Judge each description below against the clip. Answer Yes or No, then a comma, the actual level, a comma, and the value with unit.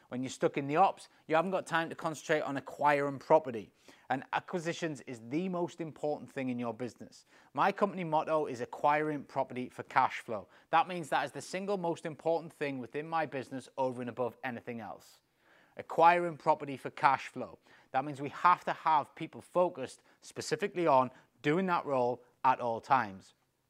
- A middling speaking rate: Yes, average, 180 wpm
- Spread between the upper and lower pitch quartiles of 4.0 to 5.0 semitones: Yes, average, 4.3 semitones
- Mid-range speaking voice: Yes, medium, 150 Hz